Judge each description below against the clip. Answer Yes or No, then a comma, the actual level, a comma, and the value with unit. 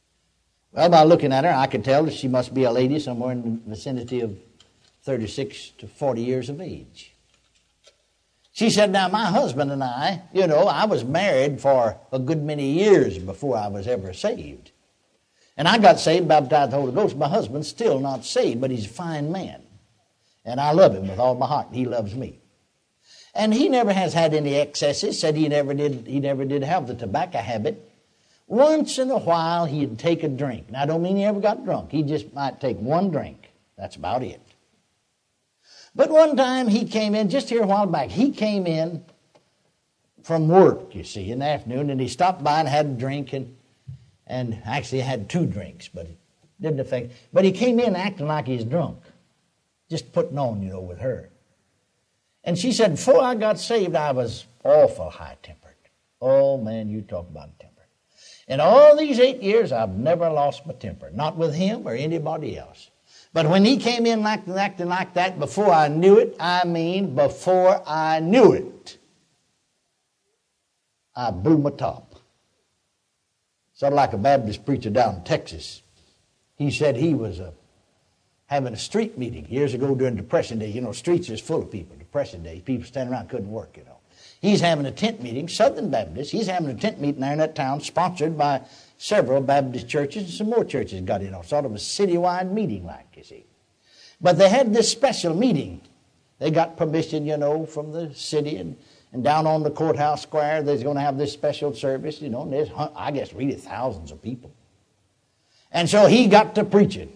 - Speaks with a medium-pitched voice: Yes, medium, 145 Hz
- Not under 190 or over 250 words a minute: Yes, average, 195 wpm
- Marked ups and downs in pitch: Yes, wide, 6.0 semitones